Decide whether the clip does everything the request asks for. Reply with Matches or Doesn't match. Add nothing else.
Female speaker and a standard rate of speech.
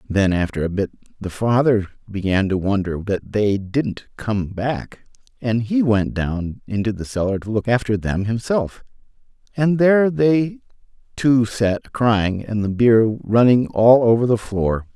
Doesn't match